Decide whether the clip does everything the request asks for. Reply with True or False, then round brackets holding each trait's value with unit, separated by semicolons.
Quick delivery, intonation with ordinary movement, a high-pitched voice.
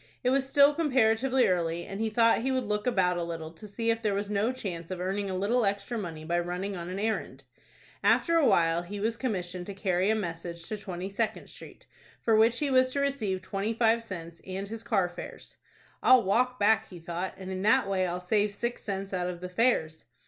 True (225 wpm; 4.2 semitones; 200 Hz)